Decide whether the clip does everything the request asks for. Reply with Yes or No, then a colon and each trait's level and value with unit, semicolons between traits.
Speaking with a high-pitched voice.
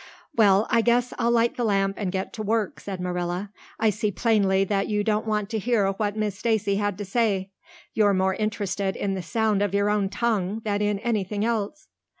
Yes: high, 205 Hz